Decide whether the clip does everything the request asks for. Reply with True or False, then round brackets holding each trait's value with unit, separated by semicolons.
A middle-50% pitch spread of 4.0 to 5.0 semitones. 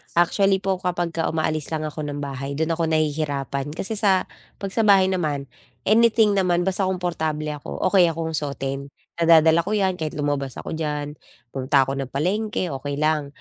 True (4.3 semitones)